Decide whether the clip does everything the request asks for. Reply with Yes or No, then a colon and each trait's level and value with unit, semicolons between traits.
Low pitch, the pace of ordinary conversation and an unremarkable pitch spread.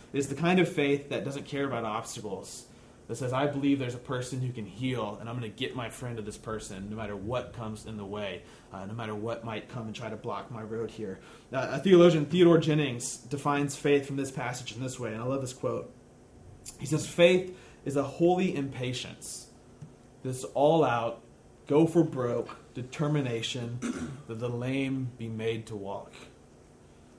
Yes: low, 125 Hz; average, 195 wpm; average, 3.8 semitones